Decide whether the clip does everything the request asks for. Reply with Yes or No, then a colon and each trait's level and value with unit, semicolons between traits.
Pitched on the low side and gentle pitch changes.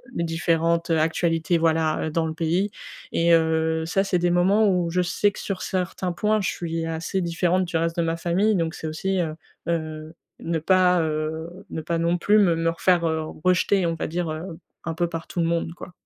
No: medium, 170 Hz; narrow, 1.8 semitones